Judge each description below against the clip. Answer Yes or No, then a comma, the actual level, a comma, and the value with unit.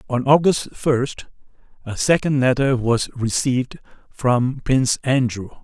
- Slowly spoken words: Yes, slow, 115 wpm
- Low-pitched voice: Yes, low, 130 Hz